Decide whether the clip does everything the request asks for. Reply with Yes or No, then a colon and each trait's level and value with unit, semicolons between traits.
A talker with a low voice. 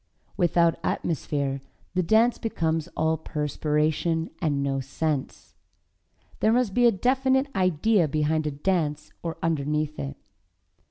No: medium, 160 Hz